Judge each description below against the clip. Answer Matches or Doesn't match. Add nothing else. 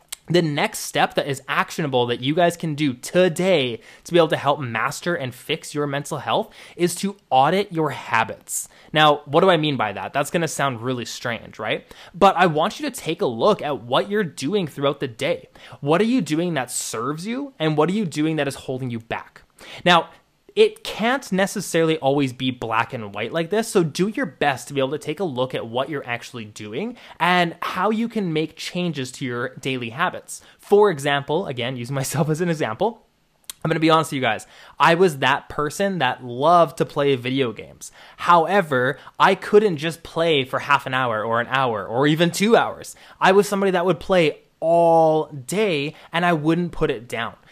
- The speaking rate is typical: Doesn't match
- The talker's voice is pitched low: Doesn't match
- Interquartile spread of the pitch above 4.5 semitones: Matches